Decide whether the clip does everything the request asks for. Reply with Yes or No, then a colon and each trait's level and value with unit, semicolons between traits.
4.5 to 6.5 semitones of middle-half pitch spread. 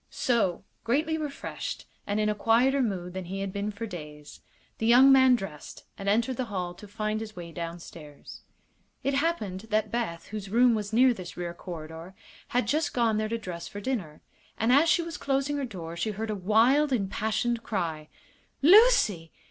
Yes: wide, 5.5 semitones